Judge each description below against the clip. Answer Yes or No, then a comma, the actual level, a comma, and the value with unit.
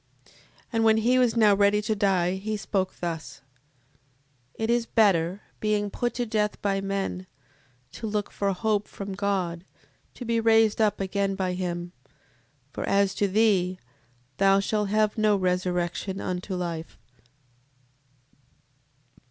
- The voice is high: Yes, high, 200 Hz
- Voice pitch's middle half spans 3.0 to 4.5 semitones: No, narrow, 2.6 semitones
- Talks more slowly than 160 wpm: Yes, average, 140 wpm